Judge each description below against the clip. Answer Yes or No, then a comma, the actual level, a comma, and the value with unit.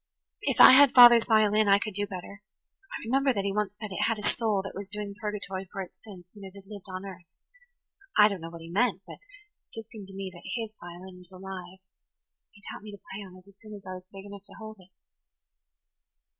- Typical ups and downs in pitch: No, narrow, 2.3 semitones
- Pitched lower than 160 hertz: No, high, 200 Hz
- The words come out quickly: Yes, fast, 240 wpm